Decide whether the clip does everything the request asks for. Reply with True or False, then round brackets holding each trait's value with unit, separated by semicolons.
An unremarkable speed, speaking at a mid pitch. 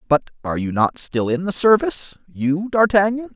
True (160 wpm; 175 Hz)